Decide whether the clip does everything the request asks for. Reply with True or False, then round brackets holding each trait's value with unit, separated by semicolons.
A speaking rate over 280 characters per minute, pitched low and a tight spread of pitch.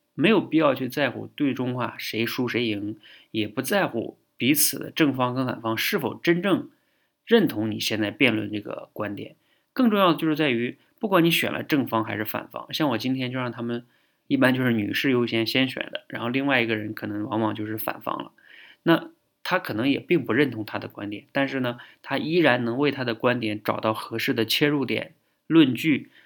False (295 characters per minute; 120 Hz; 4.8 semitones)